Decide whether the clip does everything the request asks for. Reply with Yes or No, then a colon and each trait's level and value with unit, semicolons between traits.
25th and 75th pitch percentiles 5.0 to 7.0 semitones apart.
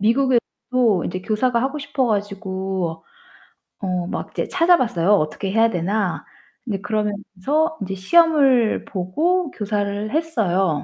Yes: wide, 5.6 semitones